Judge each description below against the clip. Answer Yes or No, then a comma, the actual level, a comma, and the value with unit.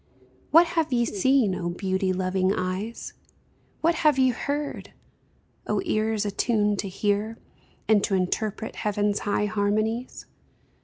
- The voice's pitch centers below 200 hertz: No, high, 210 Hz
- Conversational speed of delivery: No, slow, 125 wpm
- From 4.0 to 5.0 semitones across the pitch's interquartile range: No, average, 3.5 semitones